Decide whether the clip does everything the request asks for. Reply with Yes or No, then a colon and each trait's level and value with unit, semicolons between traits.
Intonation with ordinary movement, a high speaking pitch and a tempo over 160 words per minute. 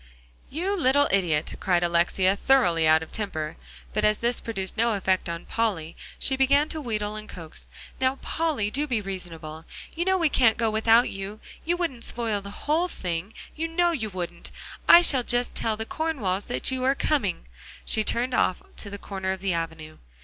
No: wide, 6.3 semitones; high, 215 Hz; average, 195 wpm